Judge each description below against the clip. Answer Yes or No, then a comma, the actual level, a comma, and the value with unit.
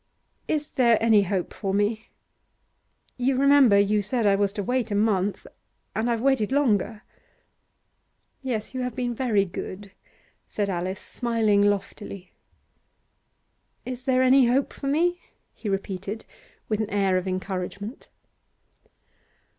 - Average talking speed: No, slow, 130 wpm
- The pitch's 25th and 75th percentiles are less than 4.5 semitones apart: Yes, average, 4.1 semitones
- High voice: Yes, high, 215 Hz